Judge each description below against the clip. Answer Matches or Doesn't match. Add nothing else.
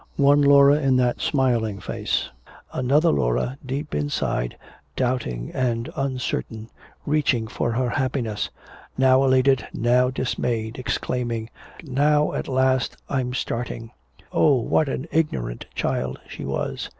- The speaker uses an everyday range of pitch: Matches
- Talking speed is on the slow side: Matches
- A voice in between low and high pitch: Doesn't match